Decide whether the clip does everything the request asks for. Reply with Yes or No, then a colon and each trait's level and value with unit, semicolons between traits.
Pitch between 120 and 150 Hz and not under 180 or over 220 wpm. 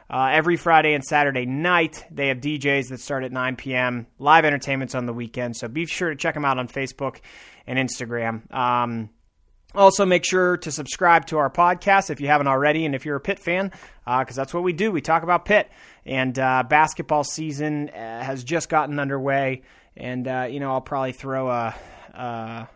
Yes: medium, 140 Hz; fast, 205 wpm